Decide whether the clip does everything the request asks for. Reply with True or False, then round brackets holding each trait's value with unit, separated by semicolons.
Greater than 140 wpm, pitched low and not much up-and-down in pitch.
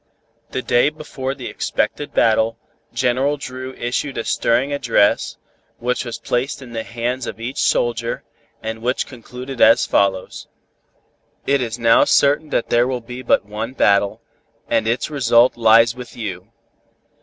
True (150 wpm; 120 Hz; 2.2 semitones)